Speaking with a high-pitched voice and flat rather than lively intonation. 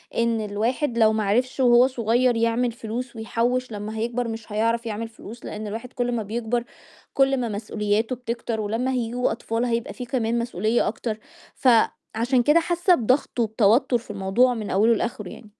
Yes: high, 230 Hz; narrow, 2.1 semitones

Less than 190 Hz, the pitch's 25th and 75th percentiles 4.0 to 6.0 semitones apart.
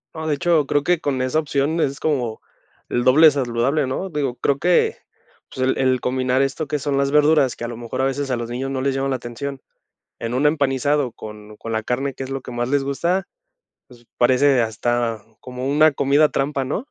No: low, 135 Hz; average, 2.7 semitones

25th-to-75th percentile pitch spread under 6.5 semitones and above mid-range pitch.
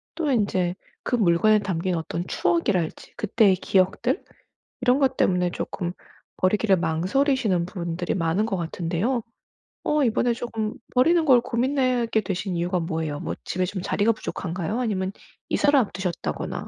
Yes: average, 5.2 semitones; high, 195 Hz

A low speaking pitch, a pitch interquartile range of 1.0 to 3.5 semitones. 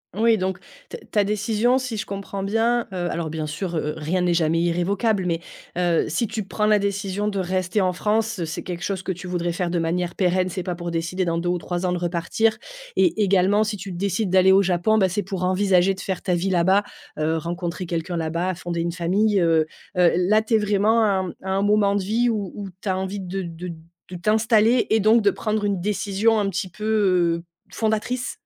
No: high, 190 Hz; average, 3.1 semitones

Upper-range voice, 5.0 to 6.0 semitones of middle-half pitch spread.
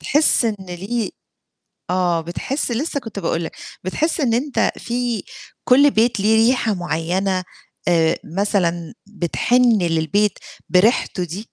Yes: high, 205 Hz; wide, 5.5 semitones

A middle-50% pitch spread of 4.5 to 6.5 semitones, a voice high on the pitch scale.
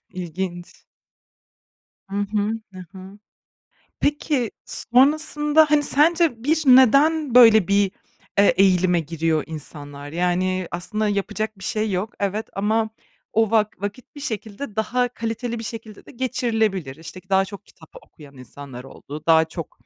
Yes: average, 5.2 semitones; high, 210 Hz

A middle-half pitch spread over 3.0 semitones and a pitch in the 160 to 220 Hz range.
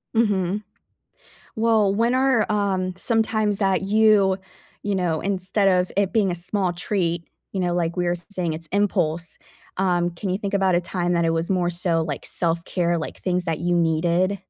No: average, 2.7 semitones; medium, 185 Hz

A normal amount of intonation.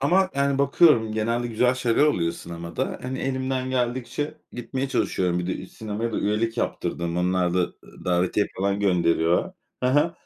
No: wide, 6.3 semitones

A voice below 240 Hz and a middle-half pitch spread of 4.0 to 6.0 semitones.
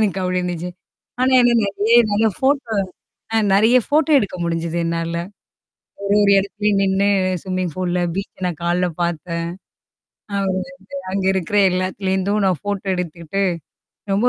No: high, 190 Hz; narrow, 2.4 semitones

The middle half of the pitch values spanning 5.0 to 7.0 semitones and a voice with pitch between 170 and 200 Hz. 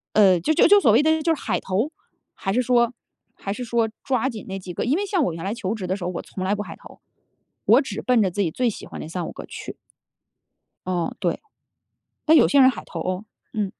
No: wide, 5.6 semitones; high, 215 Hz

